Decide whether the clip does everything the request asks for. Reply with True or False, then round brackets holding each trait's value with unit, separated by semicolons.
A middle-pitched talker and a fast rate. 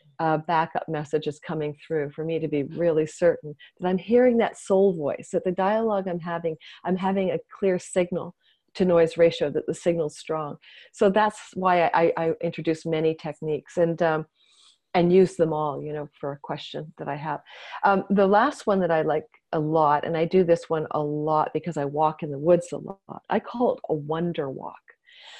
True (165 Hz; 215 wpm)